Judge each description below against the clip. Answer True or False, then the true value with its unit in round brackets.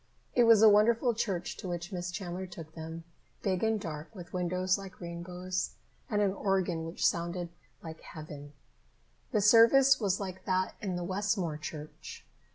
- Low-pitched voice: False (185 Hz)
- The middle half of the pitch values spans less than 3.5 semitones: True (3.1 semitones)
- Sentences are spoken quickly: False (165 wpm)